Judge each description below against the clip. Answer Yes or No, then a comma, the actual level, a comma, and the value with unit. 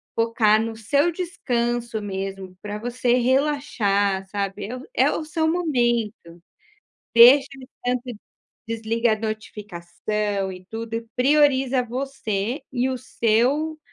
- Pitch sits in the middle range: No, high, 235 Hz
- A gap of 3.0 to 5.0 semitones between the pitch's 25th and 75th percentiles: Yes, average, 3.8 semitones